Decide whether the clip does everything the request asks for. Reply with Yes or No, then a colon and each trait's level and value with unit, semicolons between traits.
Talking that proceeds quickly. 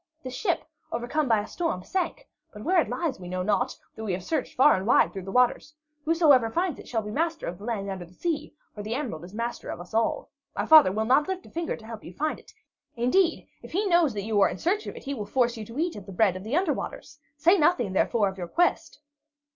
Yes: fast, 265 wpm